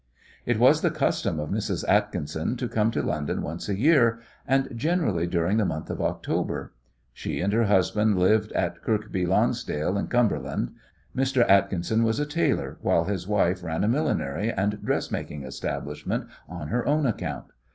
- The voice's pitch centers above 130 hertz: No, low, 105 Hz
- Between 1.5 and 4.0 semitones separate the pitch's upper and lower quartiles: No, average, 5.0 semitones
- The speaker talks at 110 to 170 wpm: Yes, average, 165 wpm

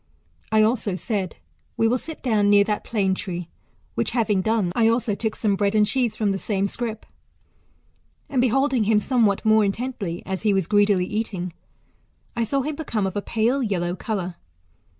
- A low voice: No, high, 215 Hz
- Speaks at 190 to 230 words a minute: No, average, 180 wpm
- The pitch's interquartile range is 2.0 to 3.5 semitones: Yes, average, 2.8 semitones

